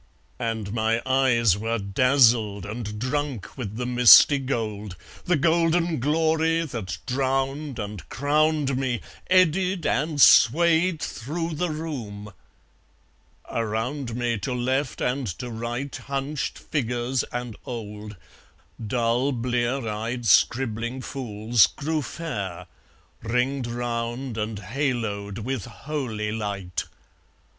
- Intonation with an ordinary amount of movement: Yes, average, 4.1 semitones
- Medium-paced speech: No, slow, 110 wpm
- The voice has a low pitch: Yes, low, 125 Hz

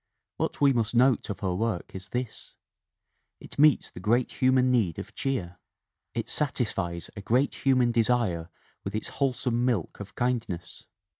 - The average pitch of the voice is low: Yes, low, 115 Hz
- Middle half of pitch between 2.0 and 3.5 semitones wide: No, average, 4.7 semitones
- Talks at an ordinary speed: Yes, average, 160 wpm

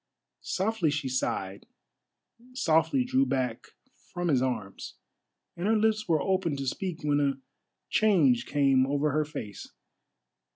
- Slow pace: Yes, slow, 130 wpm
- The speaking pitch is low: No, medium, 150 Hz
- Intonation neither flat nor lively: No, wide, 6.3 semitones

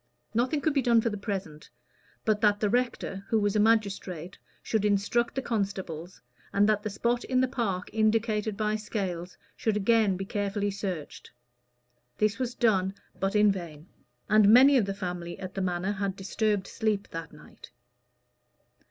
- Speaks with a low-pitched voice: No, high, 205 Hz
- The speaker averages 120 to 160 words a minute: No, average, 170 wpm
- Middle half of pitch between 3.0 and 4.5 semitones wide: No, narrow, 2.6 semitones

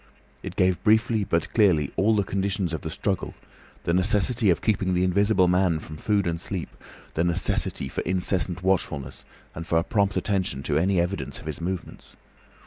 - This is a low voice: Yes, very low, 95 Hz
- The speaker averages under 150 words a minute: No, average, 180 wpm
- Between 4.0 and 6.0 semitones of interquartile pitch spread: No, average, 3.0 semitones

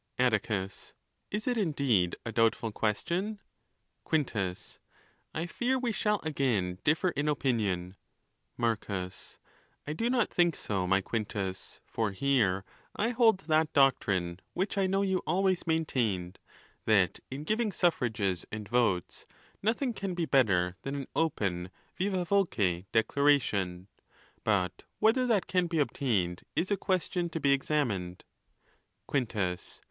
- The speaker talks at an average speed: No, slow, 125 wpm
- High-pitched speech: No, low, 135 Hz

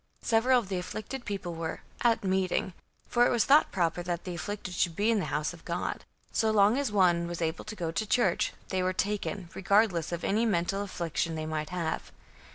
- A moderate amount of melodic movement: Yes, average, 3.9 semitones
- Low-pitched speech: No, medium, 185 Hz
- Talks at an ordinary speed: No, fast, 210 wpm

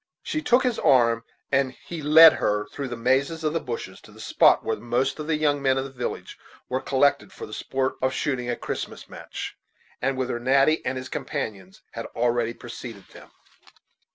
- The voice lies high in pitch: No, low, 130 Hz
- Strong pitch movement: No, average, 3.2 semitones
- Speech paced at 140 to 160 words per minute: No, average, 195 wpm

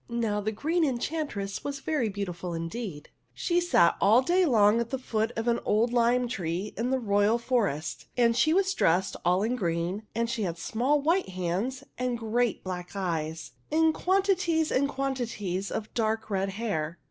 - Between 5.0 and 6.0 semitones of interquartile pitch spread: Yes, average, 5.3 semitones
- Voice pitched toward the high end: Yes, high, 225 Hz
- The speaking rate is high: No, average, 180 wpm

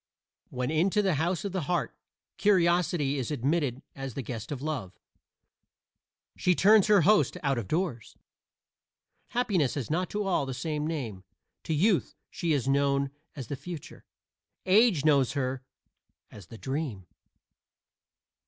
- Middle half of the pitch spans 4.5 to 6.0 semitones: Yes, average, 5.2 semitones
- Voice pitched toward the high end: No, medium, 150 Hz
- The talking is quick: No, average, 145 wpm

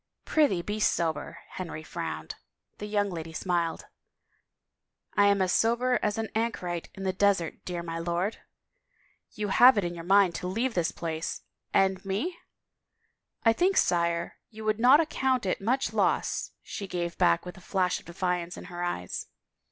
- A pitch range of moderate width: Yes, average, 3.9 semitones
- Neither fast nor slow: Yes, average, 185 wpm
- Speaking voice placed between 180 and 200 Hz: Yes, high, 190 Hz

